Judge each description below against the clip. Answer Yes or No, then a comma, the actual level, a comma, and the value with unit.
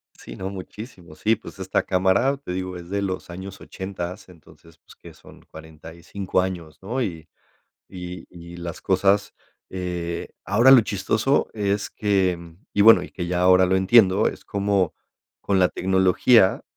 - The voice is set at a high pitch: No, very low, 95 Hz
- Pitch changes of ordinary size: No, narrow, 2.1 semitones